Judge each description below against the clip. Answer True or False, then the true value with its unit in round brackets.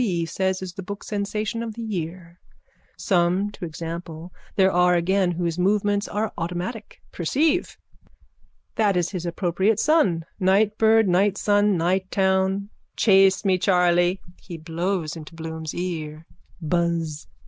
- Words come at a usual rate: False (125 wpm)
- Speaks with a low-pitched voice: False (185 Hz)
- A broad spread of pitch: False (3.0 semitones)